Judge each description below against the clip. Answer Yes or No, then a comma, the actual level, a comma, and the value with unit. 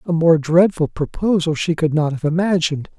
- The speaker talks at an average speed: Yes, average, 180 wpm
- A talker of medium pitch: Yes, medium, 165 Hz